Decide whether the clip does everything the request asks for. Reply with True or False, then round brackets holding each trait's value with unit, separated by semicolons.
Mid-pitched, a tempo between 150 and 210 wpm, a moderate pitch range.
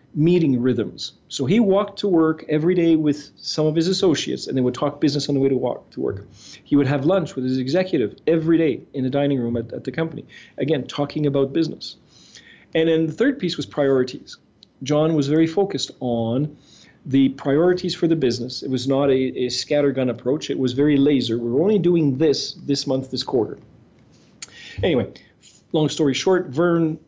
True (145 Hz; 195 wpm; 3.5 semitones)